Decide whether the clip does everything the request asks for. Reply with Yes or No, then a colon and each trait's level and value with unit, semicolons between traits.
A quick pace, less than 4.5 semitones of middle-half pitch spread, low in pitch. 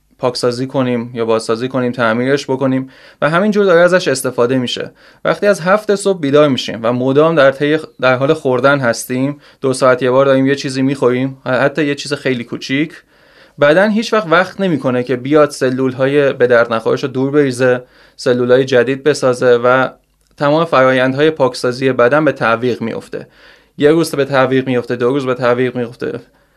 Yes: fast, 175 wpm; average, 2.7 semitones; low, 130 Hz